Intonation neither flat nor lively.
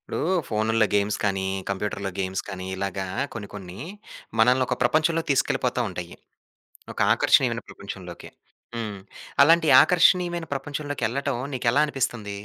No: wide, 6.1 semitones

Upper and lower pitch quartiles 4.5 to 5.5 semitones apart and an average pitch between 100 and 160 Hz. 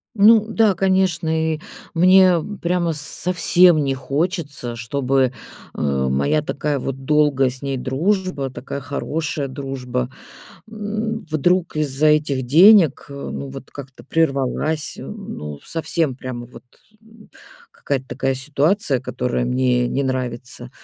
Yes: average, 4.9 semitones; medium, 140 Hz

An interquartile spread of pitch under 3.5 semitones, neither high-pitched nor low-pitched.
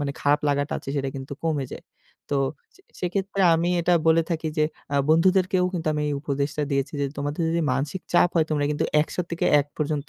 Yes: average, 3.0 semitones; medium, 150 Hz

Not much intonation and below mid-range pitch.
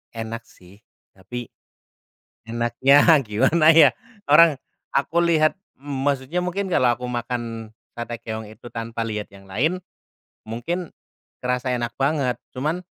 No: average, 4.8 semitones; low, 125 Hz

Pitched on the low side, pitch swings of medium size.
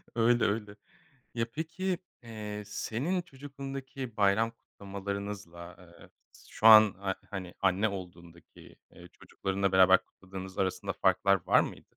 Yes: low, 100 Hz; average, 3.4 semitones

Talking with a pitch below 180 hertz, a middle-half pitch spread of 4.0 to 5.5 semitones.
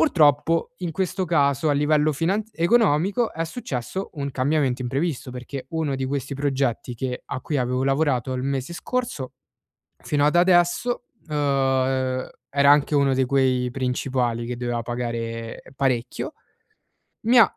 Yes: medium, 140 Hz; average, 4.3 semitones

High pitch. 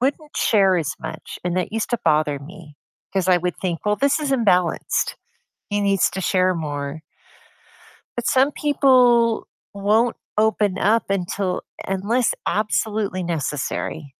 Yes: high, 195 Hz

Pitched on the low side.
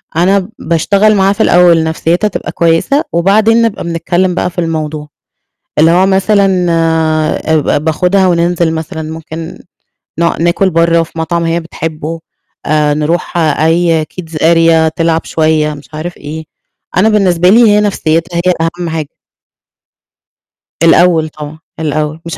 No: medium, 165 Hz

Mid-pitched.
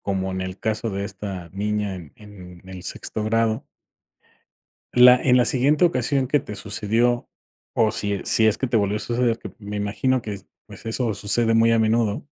No: low, 110 Hz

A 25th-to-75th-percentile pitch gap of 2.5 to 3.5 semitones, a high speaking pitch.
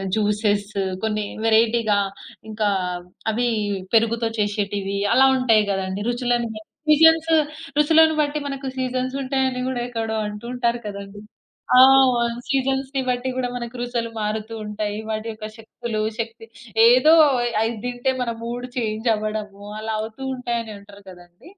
Yes: average, 3.0 semitones; high, 230 Hz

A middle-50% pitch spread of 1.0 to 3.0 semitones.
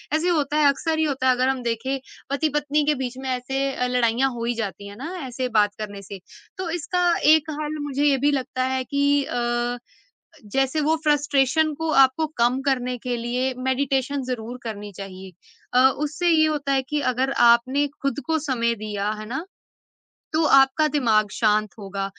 No: average, 3.7 semitones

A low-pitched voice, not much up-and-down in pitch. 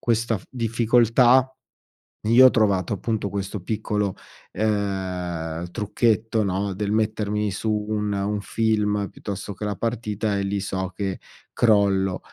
Yes: low, 105 Hz; narrow, 2.2 semitones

